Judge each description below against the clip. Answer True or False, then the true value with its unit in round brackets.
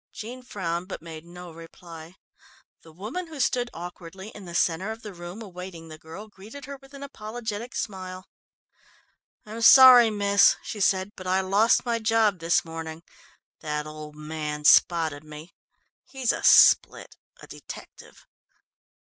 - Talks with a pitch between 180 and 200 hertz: True (185 Hz)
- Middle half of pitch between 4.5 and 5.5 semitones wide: True (5.2 semitones)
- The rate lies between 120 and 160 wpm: True (150 wpm)